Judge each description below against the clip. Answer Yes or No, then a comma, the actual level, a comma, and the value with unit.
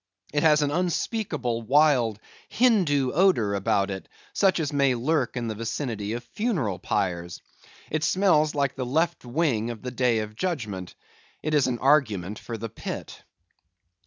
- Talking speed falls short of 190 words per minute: Yes, average, 160 wpm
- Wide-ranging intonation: Yes, wide, 5.8 semitones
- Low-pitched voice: Yes, low, 130 Hz